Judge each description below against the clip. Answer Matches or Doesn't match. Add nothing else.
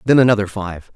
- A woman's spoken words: Doesn't match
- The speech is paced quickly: Doesn't match